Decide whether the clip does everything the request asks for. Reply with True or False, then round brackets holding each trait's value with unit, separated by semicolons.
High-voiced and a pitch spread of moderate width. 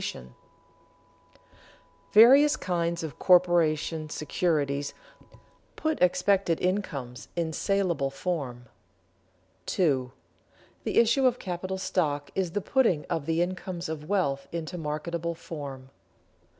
False (170 Hz; 4.1 semitones)